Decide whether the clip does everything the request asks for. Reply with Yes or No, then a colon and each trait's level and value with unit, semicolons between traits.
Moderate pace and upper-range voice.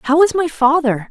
No: fast, 215 wpm; very high, 295 Hz